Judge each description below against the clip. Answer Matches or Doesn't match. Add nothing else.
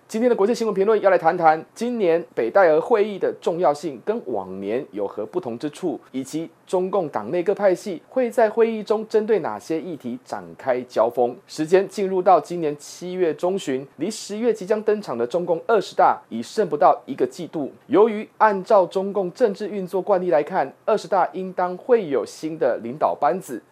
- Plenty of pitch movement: Doesn't match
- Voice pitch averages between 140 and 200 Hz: Matches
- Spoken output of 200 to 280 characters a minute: Doesn't match